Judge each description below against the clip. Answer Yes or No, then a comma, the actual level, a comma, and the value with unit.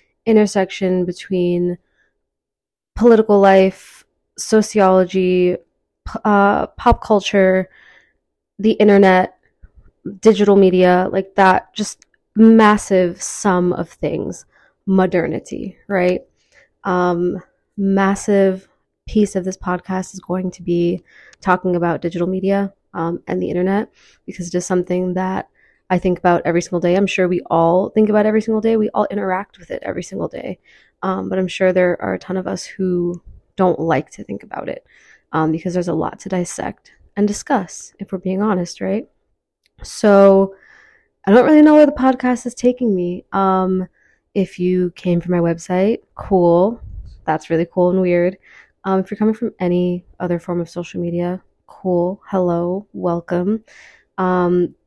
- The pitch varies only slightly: Yes, narrow, 2.3 semitones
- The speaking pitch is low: No, medium, 185 Hz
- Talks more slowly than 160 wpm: Yes, average, 150 wpm